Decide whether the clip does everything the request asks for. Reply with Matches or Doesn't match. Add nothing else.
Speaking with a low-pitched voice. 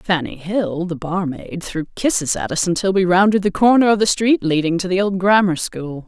Doesn't match